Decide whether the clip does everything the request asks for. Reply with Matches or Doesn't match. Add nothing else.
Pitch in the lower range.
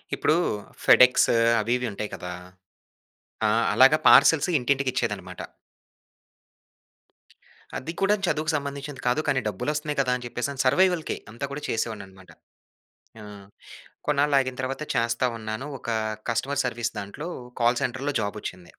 Matches